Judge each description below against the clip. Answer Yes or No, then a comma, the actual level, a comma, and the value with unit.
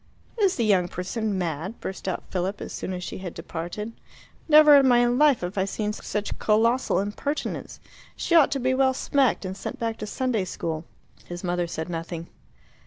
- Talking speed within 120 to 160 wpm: No, average, 185 wpm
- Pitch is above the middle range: Yes, high, 210 Hz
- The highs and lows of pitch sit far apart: Yes, wide, 6.0 semitones